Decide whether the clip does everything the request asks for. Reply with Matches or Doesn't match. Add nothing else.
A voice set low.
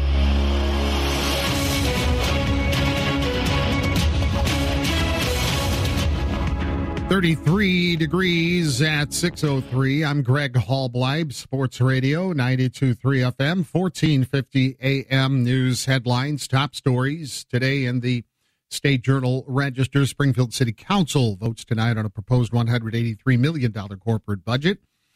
Matches